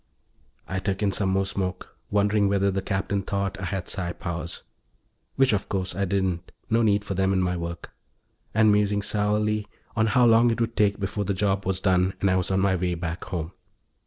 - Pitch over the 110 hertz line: No, low, 100 Hz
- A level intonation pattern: Yes, narrow, 1.8 semitones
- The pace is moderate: No, fast, 210 wpm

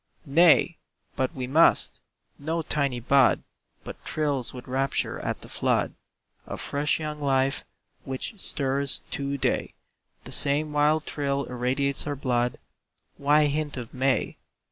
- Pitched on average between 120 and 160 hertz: Yes, medium, 140 Hz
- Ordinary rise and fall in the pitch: No, narrow, 2.2 semitones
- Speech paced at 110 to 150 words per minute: Yes, slow, 135 wpm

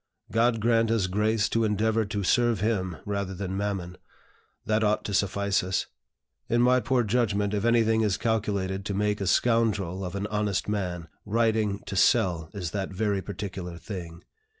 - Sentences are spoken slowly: No, average, 170 wpm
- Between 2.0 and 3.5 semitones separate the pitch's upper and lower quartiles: Yes, narrow, 2.6 semitones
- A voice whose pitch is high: No, low, 105 Hz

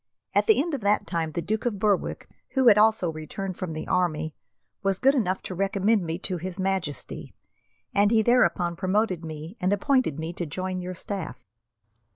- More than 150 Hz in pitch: Yes, medium, 185 Hz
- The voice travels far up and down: No, average, 3.8 semitones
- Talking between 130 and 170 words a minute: No, average, 190 wpm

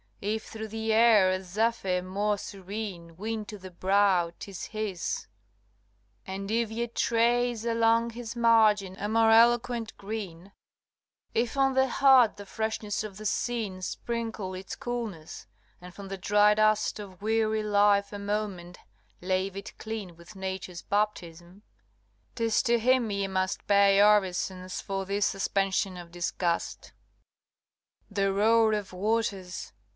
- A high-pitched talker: Yes, high, 205 Hz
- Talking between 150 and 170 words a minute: No, average, 140 wpm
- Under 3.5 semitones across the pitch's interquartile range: Yes, average, 2.9 semitones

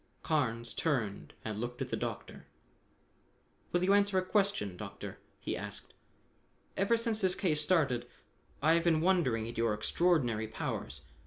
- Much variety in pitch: Yes, wide, 8.4 semitones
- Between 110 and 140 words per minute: No, average, 150 wpm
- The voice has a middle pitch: Yes, medium, 150 Hz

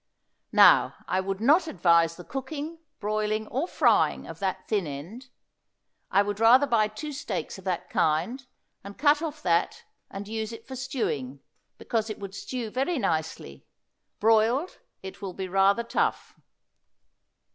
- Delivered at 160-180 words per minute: No, average, 150 wpm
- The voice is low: No, high, 215 Hz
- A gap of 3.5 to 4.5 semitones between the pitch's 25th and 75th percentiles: No, wide, 5.5 semitones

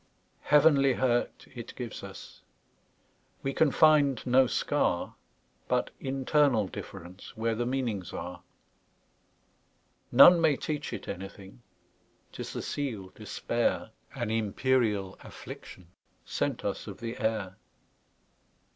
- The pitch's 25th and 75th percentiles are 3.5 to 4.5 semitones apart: No, average, 5.3 semitones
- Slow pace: Yes, slow, 90 wpm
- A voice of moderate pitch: No, low, 120 Hz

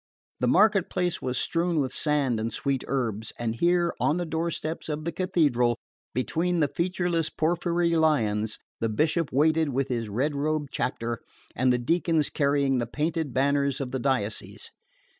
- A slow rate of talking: No, average, 160 wpm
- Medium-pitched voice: Yes, medium, 145 Hz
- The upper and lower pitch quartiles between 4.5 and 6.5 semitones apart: Yes, average, 5.0 semitones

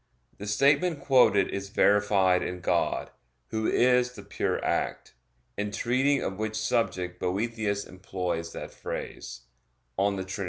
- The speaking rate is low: Yes, slow, 130 wpm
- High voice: No, low, 105 Hz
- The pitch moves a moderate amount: Yes, average, 3.9 semitones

